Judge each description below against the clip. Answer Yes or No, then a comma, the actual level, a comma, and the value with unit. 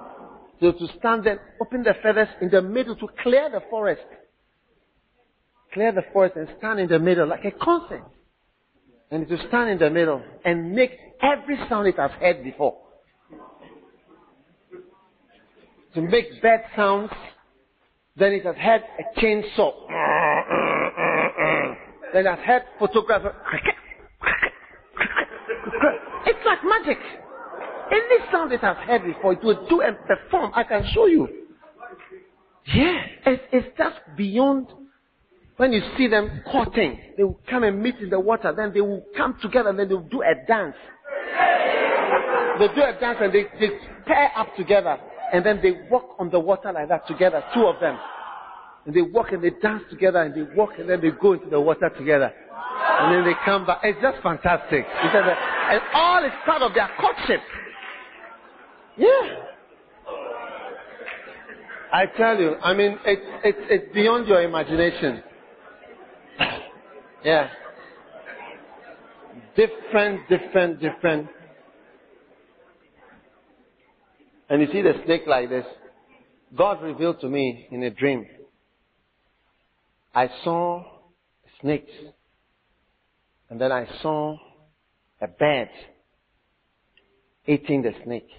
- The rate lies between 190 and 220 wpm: No, average, 140 wpm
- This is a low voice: No, high, 205 Hz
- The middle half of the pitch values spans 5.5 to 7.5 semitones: Yes, wide, 6.7 semitones